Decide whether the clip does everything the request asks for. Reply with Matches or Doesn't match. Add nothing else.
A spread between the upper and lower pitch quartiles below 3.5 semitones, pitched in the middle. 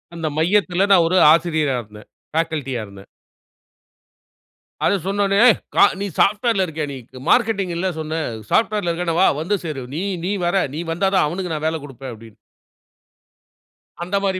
Doesn't match